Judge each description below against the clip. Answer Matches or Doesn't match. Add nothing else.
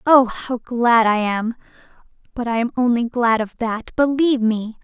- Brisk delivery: Doesn't match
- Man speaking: Doesn't match